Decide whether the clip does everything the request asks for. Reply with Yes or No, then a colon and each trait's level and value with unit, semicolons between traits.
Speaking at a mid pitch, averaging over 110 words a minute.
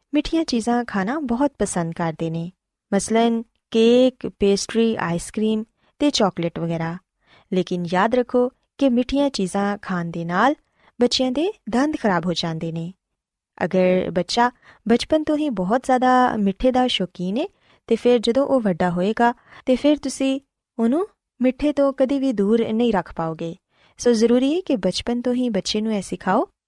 No: high, 230 Hz; average, 160 wpm